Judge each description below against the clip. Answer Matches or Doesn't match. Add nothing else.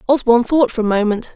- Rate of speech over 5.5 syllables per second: Matches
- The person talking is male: Doesn't match